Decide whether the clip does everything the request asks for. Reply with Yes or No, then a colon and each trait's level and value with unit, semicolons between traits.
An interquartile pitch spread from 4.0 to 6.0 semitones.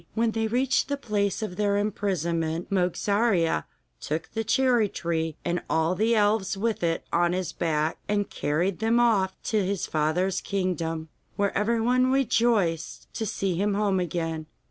Yes: average, 4.6 semitones